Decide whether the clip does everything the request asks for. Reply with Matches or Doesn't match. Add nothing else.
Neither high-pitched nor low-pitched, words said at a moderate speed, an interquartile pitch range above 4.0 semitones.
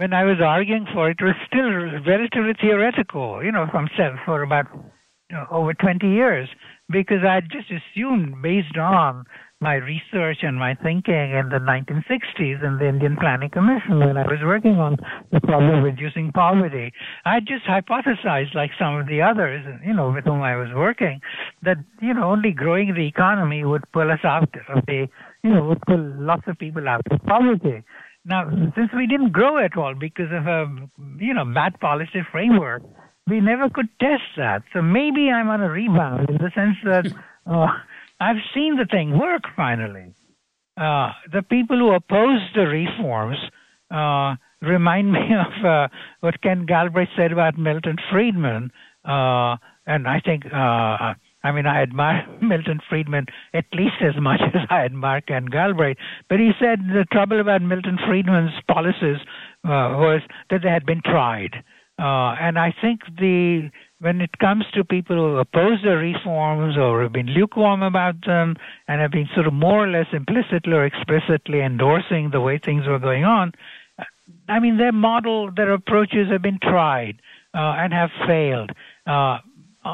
Matches